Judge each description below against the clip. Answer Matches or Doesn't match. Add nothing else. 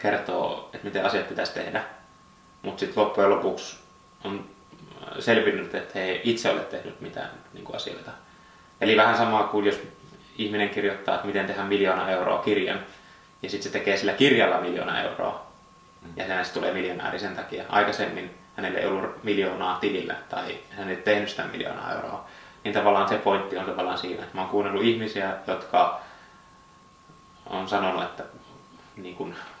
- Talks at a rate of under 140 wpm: Doesn't match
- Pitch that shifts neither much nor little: Doesn't match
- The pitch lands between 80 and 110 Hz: Matches